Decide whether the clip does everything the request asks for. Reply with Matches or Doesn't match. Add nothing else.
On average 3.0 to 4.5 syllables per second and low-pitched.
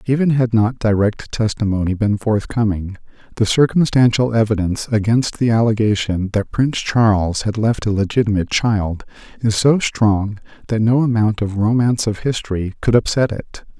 Doesn't match